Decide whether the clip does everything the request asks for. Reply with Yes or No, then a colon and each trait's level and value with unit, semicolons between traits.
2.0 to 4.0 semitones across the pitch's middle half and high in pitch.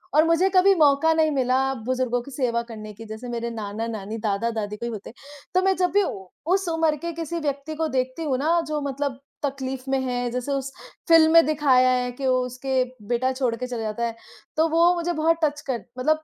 No: average, 4.7 semitones; very high, 265 Hz